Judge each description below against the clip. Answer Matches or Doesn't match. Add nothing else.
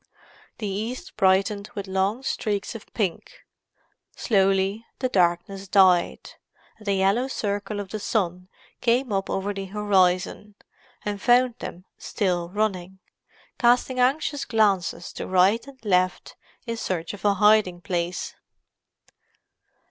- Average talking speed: Doesn't match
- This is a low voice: Doesn't match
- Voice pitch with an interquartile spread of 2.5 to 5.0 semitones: Matches